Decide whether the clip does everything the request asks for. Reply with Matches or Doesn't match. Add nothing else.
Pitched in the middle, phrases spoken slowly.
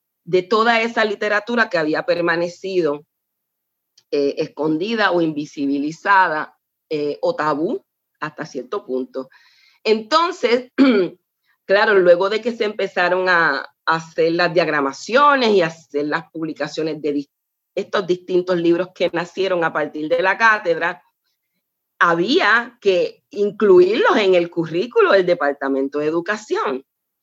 Matches